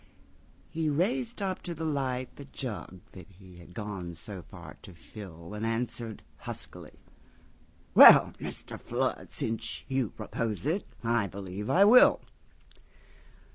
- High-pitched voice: No, low, 115 Hz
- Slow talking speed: Yes, slow, 120 wpm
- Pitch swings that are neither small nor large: No, wide, 7.3 semitones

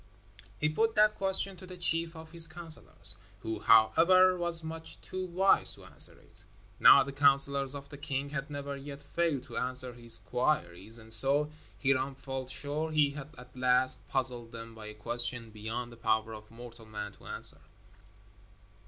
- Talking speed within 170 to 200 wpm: Yes, average, 175 wpm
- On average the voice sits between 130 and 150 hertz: Yes, low, 135 Hz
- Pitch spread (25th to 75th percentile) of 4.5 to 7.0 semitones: Yes, wide, 5.4 semitones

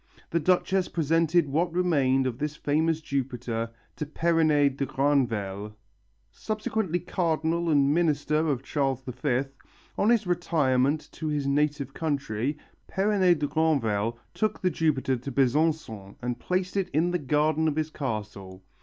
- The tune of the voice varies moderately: Yes, average, 4.0 semitones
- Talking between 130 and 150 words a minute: Yes, average, 140 wpm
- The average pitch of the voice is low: No, medium, 150 Hz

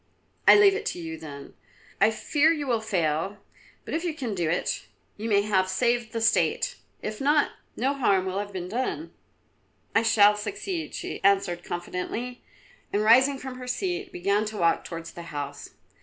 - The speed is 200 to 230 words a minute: No, average, 180 wpm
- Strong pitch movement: Yes, wide, 6.2 semitones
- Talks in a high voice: Yes, high, 215 Hz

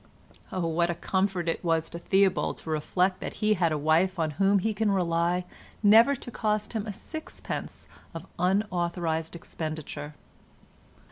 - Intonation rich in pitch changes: No, average, 3.4 semitones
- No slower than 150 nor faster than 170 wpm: Yes, average, 155 wpm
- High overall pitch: No, medium, 180 Hz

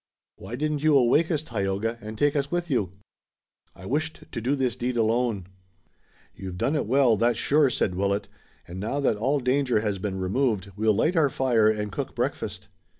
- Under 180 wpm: No, average, 190 wpm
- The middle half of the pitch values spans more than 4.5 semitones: Yes, average, 5.3 semitones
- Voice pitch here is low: Yes, low, 120 Hz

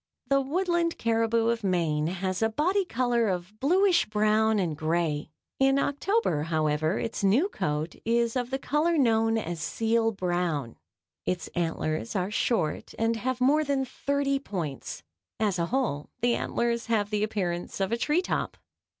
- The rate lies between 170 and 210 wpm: No, average, 160 wpm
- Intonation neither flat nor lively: No, wide, 7.2 semitones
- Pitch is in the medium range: No, high, 225 Hz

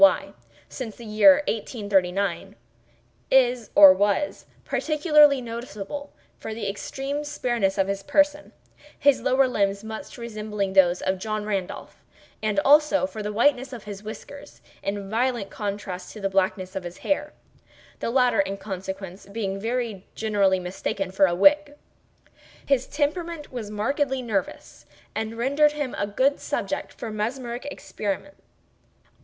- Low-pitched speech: No, high, 220 Hz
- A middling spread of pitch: No, wide, 5.7 semitones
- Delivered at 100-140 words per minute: Yes, slow, 135 wpm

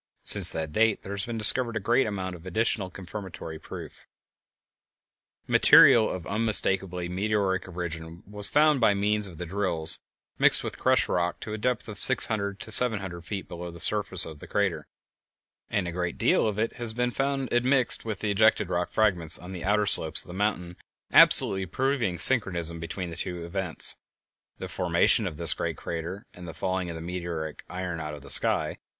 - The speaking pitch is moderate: No, very low, 95 Hz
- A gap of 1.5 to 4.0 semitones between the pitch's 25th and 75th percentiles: Yes, average, 3.7 semitones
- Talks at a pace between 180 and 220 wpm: Yes, average, 190 wpm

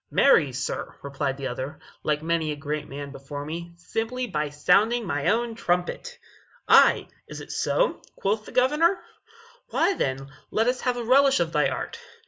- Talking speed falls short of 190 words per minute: Yes, average, 170 wpm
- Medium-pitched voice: Yes, medium, 170 Hz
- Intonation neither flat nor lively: No, wide, 8.9 semitones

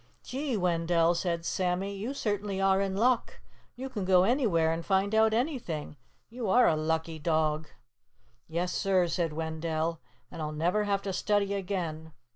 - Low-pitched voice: No, medium, 185 Hz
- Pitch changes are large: No, average, 3.9 semitones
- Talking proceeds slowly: No, average, 160 wpm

